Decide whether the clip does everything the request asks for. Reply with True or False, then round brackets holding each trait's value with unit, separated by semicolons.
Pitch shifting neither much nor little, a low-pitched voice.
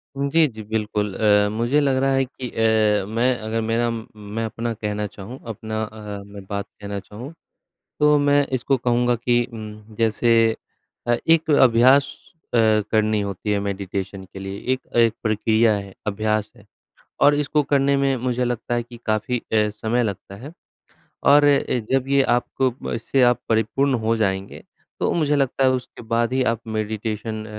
True (3.5 semitones; 115 Hz)